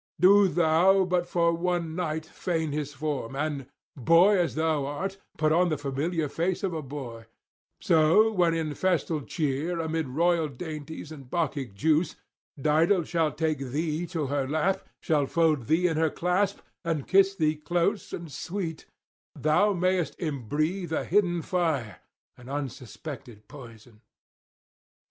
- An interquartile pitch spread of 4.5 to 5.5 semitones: No, average, 3.3 semitones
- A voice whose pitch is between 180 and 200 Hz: No, medium, 160 Hz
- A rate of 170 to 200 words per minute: No, average, 145 wpm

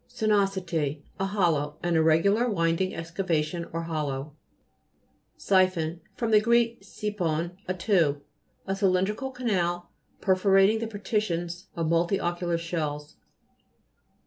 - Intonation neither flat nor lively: Yes, average, 3.2 semitones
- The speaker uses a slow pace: Yes, slow, 100 wpm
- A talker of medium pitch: Yes, medium, 175 Hz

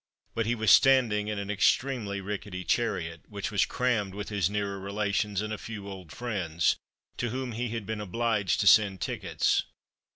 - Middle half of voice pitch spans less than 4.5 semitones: Yes, narrow, 2.5 semitones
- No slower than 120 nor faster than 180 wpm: Yes, average, 175 wpm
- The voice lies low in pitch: Yes, low, 105 Hz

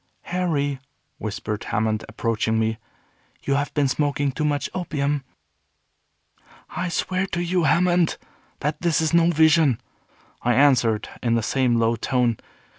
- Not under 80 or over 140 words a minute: Yes, slow, 135 wpm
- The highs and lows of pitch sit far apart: Yes, wide, 5.7 semitones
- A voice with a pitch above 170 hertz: No, medium, 140 Hz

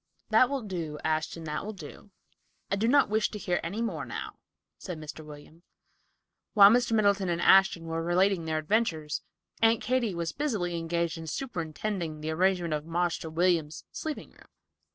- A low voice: No, medium, 175 Hz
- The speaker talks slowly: No, average, 170 wpm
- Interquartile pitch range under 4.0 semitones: No, average, 4.7 semitones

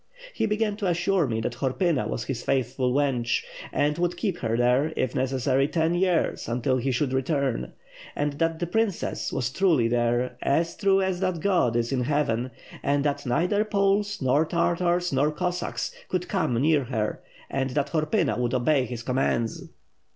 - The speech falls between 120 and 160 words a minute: No, average, 175 wpm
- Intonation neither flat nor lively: No, wide, 5.7 semitones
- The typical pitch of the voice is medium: Yes, medium, 145 Hz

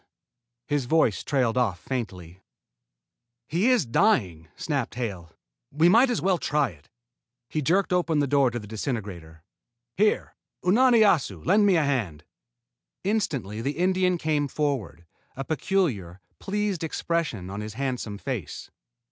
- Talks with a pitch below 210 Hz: Yes, medium, 140 Hz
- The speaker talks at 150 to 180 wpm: No, slow, 135 wpm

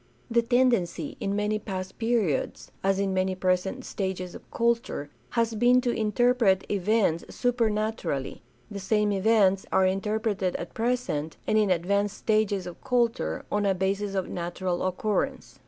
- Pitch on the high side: Yes, high, 200 Hz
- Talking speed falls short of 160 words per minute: Yes, average, 150 wpm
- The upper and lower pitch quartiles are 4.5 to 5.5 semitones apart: No, average, 3.3 semitones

